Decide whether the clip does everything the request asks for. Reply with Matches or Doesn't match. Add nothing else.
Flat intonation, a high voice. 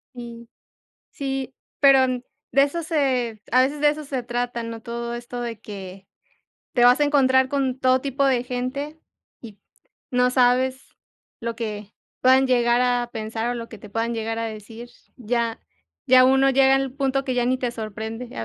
Matches